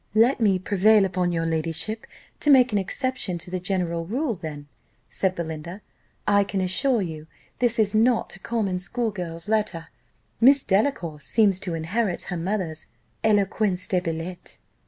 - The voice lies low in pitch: No, high, 190 Hz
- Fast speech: No, average, 155 wpm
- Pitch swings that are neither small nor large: Yes, average, 4.4 semitones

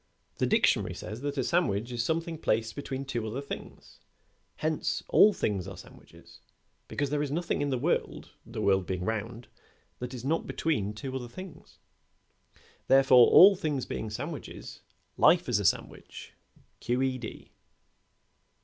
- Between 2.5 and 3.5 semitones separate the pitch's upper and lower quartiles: No, average, 5.1 semitones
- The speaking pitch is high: No, low, 130 Hz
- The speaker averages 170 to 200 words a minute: No, average, 155 wpm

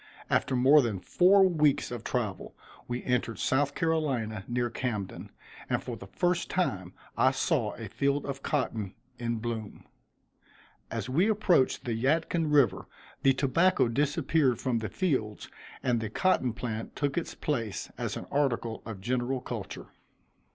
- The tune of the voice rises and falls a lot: No, average, 4.6 semitones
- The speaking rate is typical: Yes, average, 150 wpm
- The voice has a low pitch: Yes, low, 130 Hz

